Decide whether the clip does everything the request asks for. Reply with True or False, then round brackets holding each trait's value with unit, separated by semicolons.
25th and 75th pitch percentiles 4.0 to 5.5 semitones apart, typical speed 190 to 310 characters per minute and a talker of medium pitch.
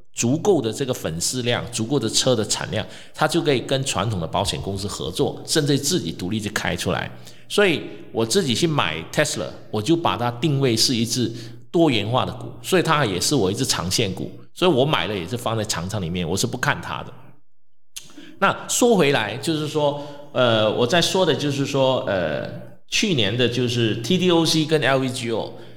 False (5.2 semitones; 285 characters per minute; 125 Hz)